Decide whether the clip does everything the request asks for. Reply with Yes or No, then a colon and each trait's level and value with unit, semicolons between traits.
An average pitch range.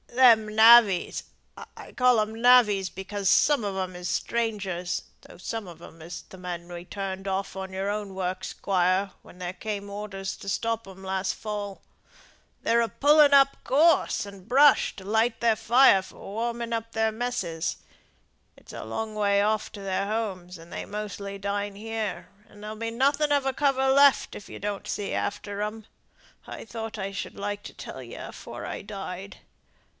Yes: average, 3.0 semitones